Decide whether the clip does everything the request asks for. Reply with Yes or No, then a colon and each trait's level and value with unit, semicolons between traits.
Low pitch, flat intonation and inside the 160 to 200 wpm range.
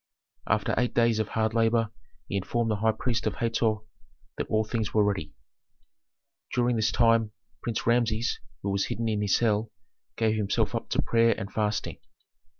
Yes: low, 110 Hz; narrow, 1.6 semitones; average, 170 wpm